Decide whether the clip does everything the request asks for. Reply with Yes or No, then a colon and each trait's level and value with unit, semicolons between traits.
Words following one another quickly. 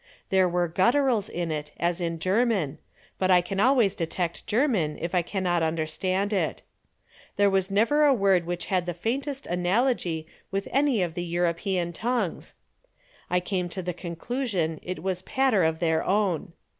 No: average, 170 wpm